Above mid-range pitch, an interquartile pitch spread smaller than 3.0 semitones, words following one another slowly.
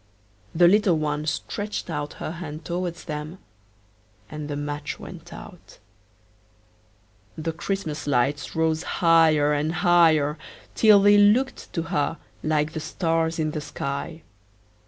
No: medium, 160 Hz; narrow, 2.6 semitones; slow, 130 wpm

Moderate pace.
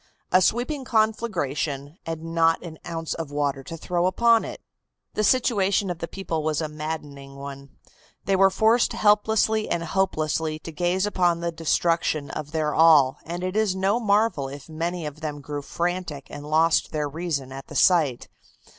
Yes: average, 170 wpm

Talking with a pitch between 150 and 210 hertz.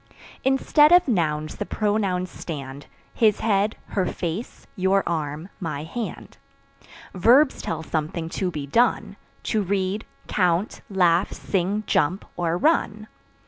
Yes: high, 190 Hz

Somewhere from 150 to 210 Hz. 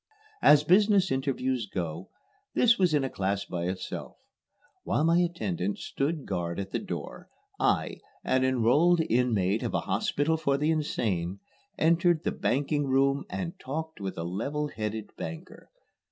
No: low, 135 Hz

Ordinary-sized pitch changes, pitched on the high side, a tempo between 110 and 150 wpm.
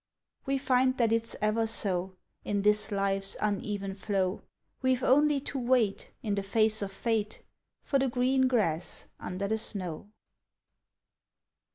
Yes: average, 4.2 semitones; high, 215 Hz; average, 140 wpm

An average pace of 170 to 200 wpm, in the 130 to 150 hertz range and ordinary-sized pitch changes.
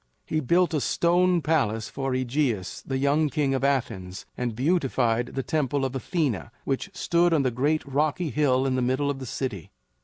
Yes: average, 185 wpm; low, 135 Hz; average, 3.4 semitones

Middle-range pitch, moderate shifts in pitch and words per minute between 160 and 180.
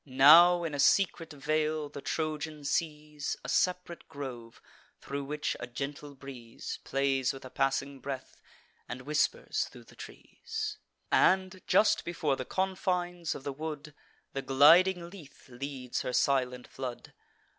No: medium, 145 Hz; average, 3.9 semitones; average, 140 wpm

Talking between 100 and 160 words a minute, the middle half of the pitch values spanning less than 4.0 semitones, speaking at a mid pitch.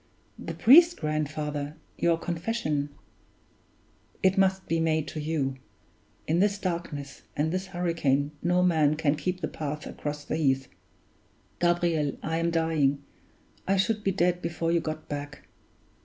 Yes: average, 145 wpm; average, 3.2 semitones; medium, 160 Hz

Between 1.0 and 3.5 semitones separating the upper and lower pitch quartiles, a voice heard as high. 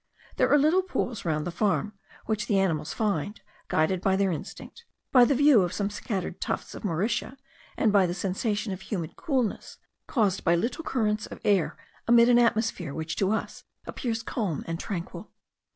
No: average, 4.4 semitones; high, 205 Hz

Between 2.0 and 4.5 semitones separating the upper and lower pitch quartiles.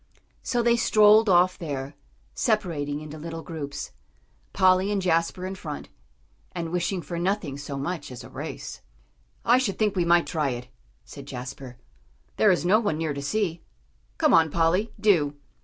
No: average, 5.2 semitones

